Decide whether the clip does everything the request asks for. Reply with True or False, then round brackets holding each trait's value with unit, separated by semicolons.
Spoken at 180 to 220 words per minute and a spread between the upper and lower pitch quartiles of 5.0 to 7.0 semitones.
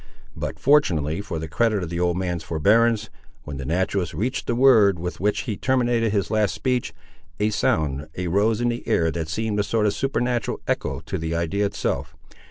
True (190 wpm; 5.5 semitones)